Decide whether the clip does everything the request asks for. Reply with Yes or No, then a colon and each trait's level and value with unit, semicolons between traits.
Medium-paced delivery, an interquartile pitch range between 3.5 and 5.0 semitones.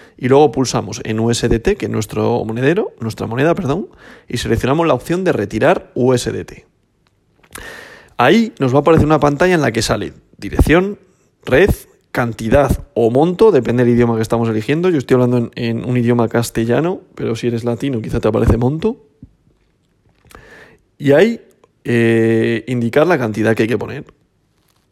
Yes: average, 160 wpm; average, 4.0 semitones